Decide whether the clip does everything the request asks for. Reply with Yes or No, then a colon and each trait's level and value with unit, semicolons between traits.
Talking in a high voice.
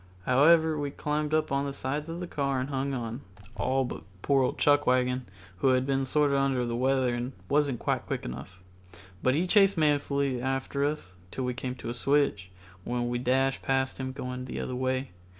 No: low, 135 Hz